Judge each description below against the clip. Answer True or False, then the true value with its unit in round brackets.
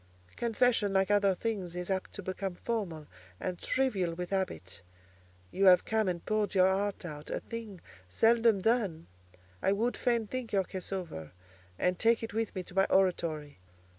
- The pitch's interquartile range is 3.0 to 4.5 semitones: True (3.7 semitones)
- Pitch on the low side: False (195 Hz)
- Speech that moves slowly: False (170 wpm)